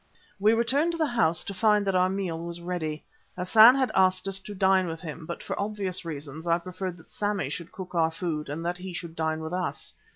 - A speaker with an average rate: No, fast, 230 wpm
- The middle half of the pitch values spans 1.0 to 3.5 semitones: Yes, average, 3.2 semitones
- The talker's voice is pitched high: No, medium, 180 Hz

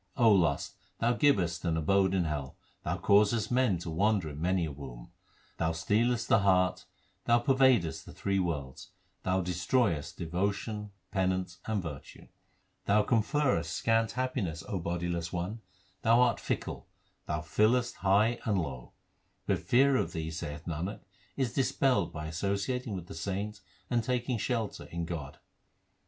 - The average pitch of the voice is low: Yes, very low, 95 Hz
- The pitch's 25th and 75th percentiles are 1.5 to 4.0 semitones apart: No, wide, 5.6 semitones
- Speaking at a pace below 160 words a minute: Yes, average, 150 wpm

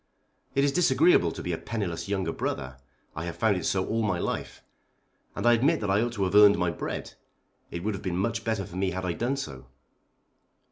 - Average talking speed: No, fast, 225 wpm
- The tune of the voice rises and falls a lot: No, average, 4.2 semitones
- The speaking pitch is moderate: No, low, 100 Hz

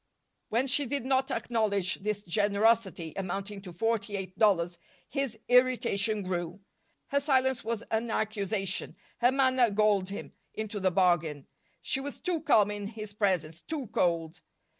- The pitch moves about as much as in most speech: Yes, average, 4.1 semitones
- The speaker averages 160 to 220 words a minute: No, average, 145 wpm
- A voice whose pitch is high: Yes, high, 210 Hz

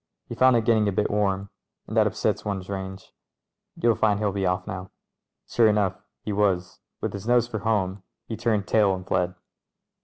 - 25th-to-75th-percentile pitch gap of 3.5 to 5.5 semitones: No, narrow, 2.5 semitones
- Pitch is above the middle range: No, low, 100 Hz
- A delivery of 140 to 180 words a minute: No, fast, 205 wpm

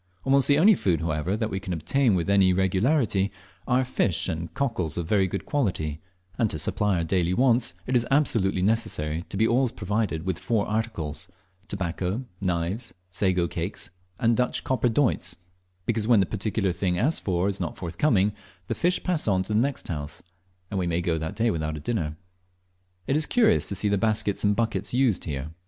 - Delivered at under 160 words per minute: No, average, 195 wpm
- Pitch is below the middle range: Yes, low, 100 Hz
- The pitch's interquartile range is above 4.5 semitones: Yes, average, 5.2 semitones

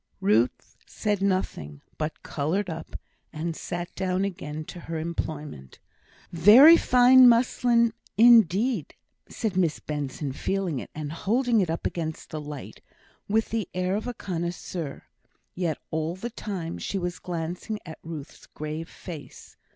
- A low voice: No, medium, 175 Hz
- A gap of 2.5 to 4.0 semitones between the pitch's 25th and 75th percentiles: No, average, 4.9 semitones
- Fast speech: No, average, 140 wpm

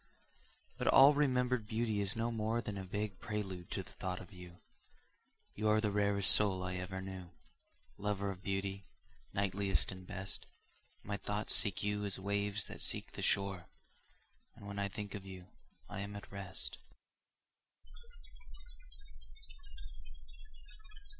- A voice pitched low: Yes, low, 100 Hz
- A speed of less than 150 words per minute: Yes, average, 140 wpm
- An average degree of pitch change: No, narrow, 1.6 semitones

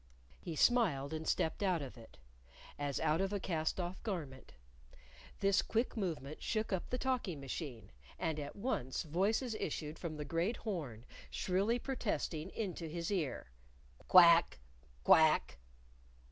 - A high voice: No, medium, 170 Hz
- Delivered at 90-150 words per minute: Yes, average, 140 wpm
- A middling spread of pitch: Yes, average, 5.0 semitones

